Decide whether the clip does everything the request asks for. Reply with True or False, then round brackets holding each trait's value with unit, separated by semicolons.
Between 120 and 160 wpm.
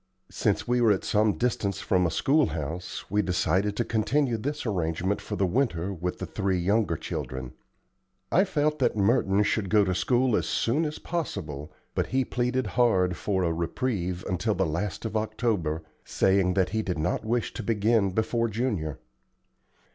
False (170 wpm)